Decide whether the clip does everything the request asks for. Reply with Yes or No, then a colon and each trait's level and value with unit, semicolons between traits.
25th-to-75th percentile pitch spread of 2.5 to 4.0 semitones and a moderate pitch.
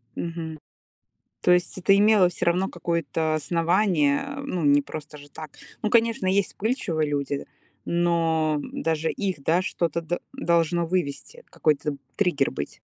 Yes: average, 3.3 semitones; medium, 170 Hz